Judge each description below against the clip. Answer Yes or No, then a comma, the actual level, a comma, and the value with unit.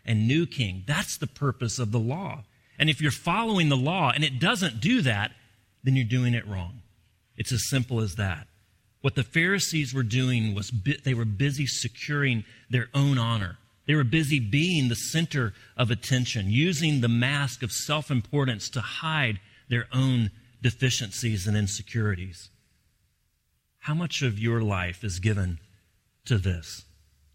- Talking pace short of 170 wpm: Yes, average, 160 wpm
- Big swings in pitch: No, average, 4.7 semitones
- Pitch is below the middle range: Yes, low, 120 Hz